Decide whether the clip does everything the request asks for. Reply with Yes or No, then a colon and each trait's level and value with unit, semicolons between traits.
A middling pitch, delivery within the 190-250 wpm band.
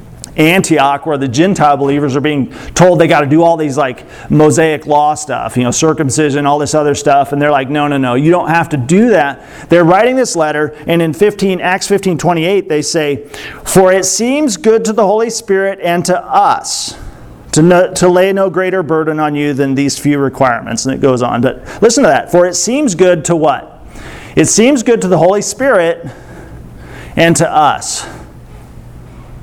Yes: medium, 165 Hz; average, 200 wpm